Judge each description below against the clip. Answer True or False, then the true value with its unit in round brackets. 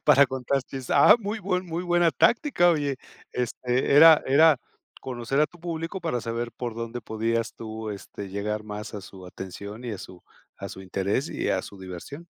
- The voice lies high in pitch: False (125 Hz)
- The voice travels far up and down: True (7.0 semitones)